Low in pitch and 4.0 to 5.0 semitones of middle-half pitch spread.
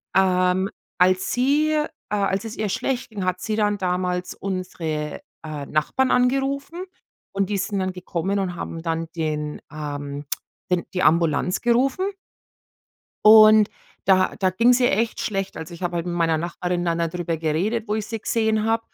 No: medium, 185 Hz; average, 4.4 semitones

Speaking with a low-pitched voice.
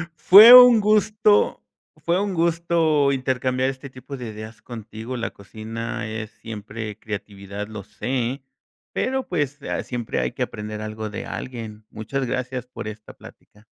Yes: low, 125 Hz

